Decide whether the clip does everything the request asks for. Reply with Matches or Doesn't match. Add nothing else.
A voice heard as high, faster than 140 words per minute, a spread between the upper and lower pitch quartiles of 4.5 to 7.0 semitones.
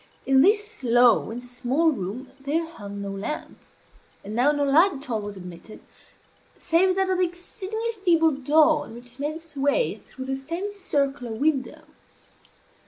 Matches